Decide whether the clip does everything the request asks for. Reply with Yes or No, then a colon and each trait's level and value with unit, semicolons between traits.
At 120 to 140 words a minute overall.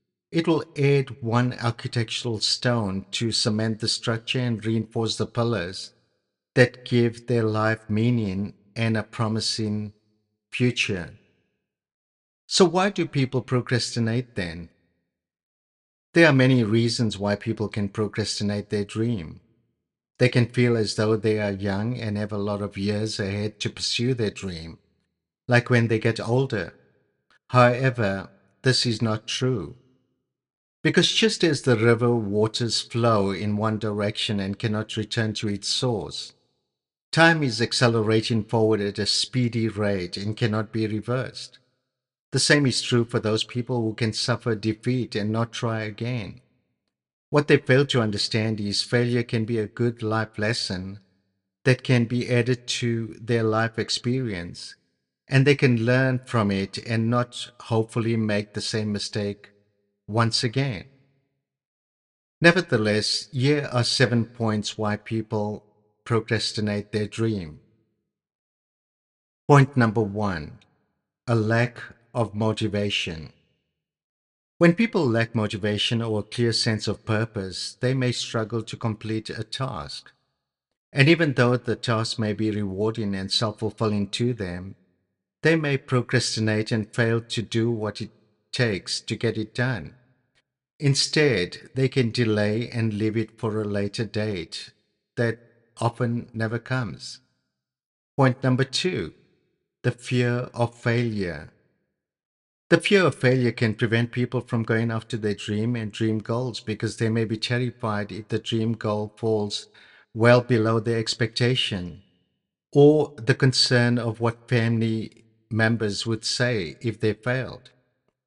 Yes: slow, 135 wpm